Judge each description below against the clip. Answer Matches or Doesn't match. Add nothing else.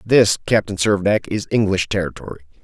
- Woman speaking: Doesn't match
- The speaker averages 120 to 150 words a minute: Matches